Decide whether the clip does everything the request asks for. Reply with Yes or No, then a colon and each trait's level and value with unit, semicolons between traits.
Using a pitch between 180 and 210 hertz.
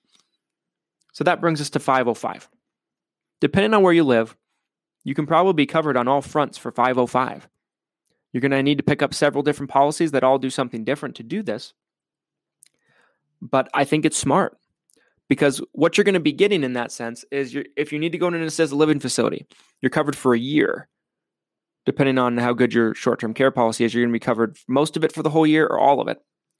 No: medium, 140 Hz